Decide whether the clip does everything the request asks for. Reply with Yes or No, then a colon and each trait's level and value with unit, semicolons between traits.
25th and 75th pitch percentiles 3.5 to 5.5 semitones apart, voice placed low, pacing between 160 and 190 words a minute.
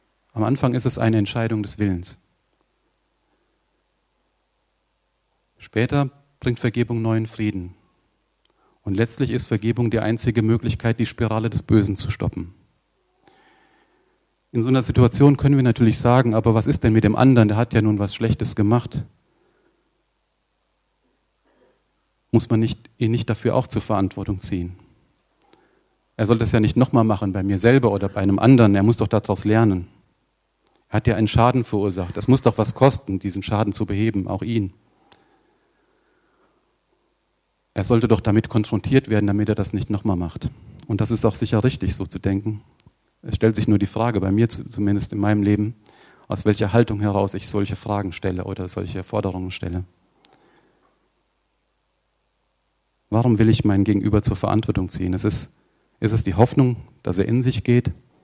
No: average, 2.8 semitones; low, 110 Hz; average, 165 wpm